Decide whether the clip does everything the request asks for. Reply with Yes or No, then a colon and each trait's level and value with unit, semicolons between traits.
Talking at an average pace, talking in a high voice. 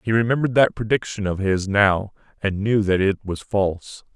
No: average, 190 wpm; low, 105 Hz